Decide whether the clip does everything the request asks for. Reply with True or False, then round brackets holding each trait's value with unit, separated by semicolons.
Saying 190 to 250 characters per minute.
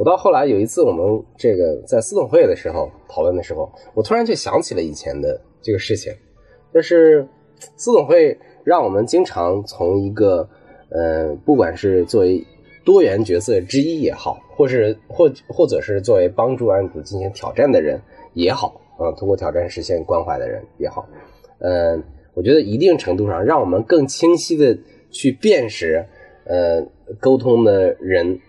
False (260 characters per minute)